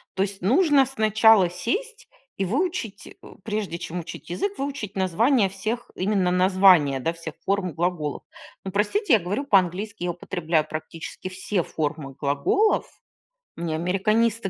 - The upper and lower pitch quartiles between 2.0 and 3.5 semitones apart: No, average, 4.6 semitones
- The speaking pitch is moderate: No, high, 195 Hz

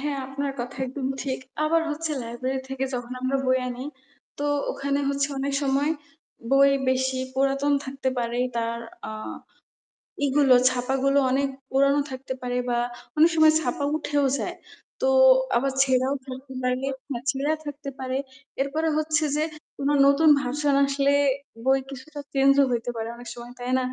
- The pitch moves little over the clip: Yes, narrow, 1.6 semitones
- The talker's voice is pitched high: Yes, very high, 270 Hz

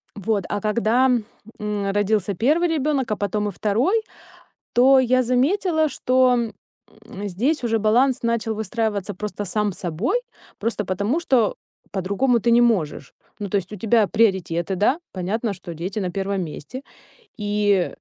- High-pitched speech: Yes, high, 215 Hz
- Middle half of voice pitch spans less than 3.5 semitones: No, average, 3.9 semitones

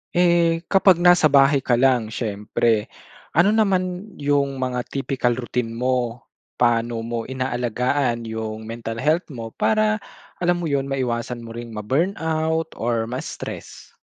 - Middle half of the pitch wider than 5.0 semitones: Yes, wide, 5.6 semitones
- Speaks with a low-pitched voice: Yes, low, 130 Hz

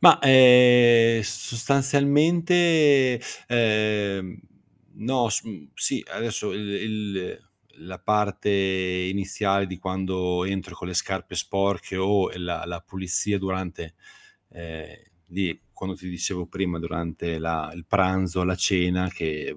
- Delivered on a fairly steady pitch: No, average, 3.7 semitones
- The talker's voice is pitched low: Yes, very low, 95 Hz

